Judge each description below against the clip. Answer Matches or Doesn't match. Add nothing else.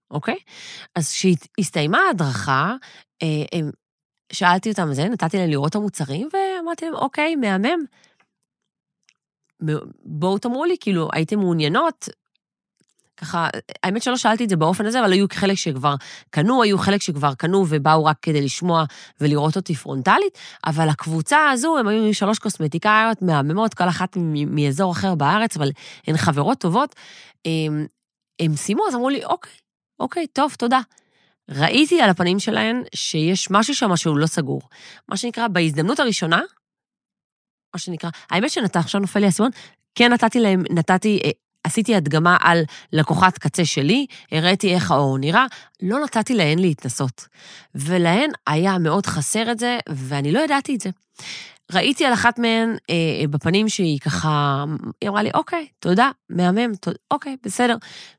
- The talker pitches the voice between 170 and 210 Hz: Matches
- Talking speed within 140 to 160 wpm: Matches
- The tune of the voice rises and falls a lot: Matches